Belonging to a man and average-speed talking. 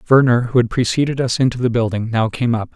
No: male; fast, 240 wpm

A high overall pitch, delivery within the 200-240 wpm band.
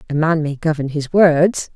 No: medium, 155 Hz; fast, 205 wpm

